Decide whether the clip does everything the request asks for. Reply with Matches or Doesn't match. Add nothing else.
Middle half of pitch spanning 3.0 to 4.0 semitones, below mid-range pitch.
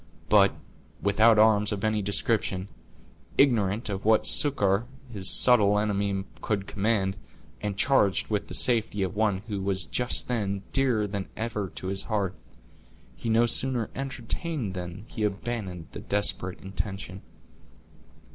Doesn't match